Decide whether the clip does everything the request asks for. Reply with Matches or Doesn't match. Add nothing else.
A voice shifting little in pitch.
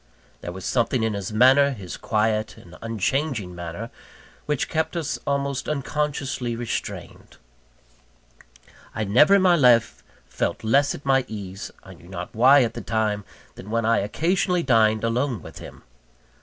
Doesn't match